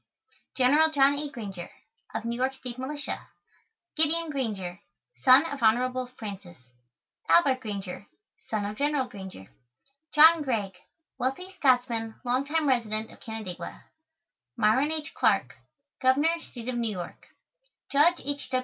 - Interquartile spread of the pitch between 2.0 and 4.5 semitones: No, average, 5.1 semitones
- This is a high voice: Yes, very high, 255 Hz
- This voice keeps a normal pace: No, slow, 130 wpm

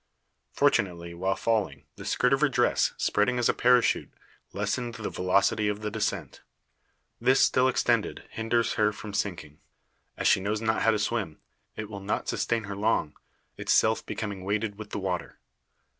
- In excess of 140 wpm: Yes, average, 165 wpm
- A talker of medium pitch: No, low, 105 Hz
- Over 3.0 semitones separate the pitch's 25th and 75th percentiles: No, narrow, 2.6 semitones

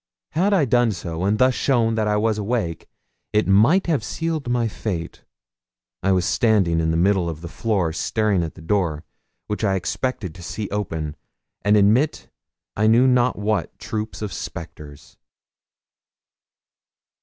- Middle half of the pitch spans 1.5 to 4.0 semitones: No, average, 5.1 semitones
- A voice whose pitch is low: Yes, low, 105 Hz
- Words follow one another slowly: No, average, 155 wpm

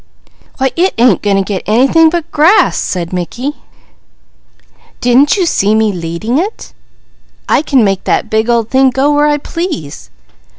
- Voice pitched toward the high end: Yes, high, 245 Hz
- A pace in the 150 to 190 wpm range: Yes, average, 160 wpm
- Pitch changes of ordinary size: No, wide, 6.6 semitones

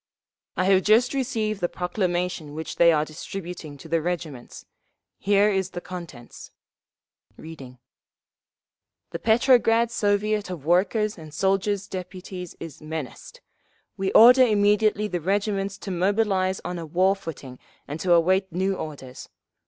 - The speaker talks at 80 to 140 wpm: Yes, slow, 135 wpm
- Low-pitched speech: No, medium, 185 Hz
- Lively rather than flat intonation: No, average, 3.7 semitones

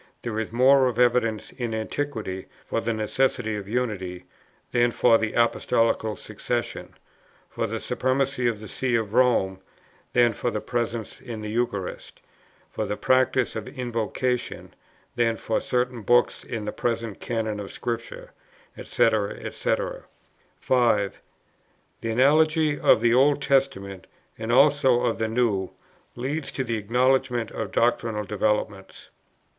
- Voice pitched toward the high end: No, low, 120 Hz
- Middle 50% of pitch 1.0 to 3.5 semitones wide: Yes, average, 2.8 semitones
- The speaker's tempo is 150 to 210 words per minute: No, average, 140 wpm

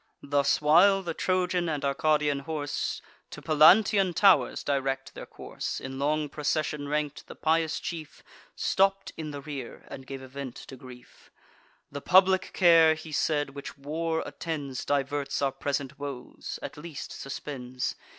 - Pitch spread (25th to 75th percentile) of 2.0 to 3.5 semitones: Yes, average, 2.8 semitones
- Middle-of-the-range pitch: Yes, medium, 150 Hz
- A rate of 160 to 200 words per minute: No, average, 150 wpm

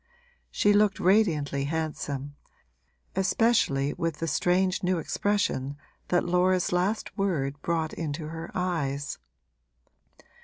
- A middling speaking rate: No, slow, 105 wpm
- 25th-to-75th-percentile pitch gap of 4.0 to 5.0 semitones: Yes, average, 4.3 semitones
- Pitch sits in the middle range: Yes, medium, 170 Hz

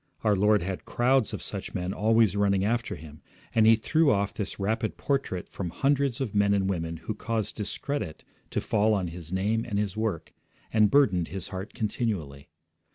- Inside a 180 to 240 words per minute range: Yes, average, 185 wpm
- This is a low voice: Yes, low, 105 Hz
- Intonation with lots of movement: No, average, 3.2 semitones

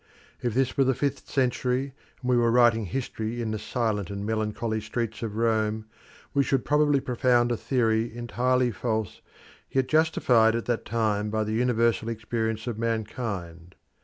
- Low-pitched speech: Yes, low, 115 Hz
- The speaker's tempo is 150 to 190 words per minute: Yes, average, 160 wpm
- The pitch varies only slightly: Yes, narrow, 2.3 semitones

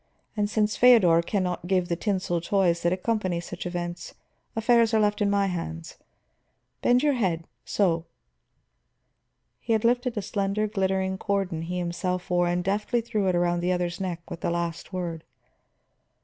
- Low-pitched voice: No, medium, 185 Hz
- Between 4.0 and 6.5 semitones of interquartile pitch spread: No, average, 3.2 semitones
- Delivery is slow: No, average, 165 wpm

